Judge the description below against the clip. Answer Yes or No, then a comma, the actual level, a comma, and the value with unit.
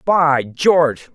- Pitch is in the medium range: Yes, medium, 150 Hz